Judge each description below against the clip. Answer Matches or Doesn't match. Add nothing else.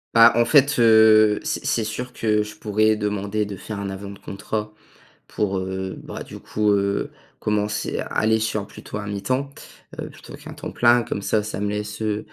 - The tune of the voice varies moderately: Doesn't match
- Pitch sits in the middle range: Doesn't match